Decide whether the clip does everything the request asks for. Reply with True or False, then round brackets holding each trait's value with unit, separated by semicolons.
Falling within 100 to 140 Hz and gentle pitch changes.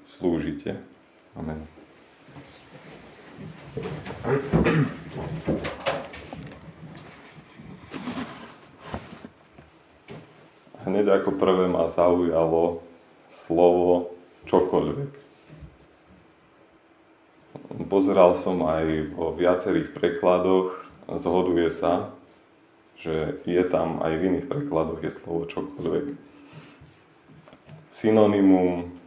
False (90 Hz; 1.9 semitones)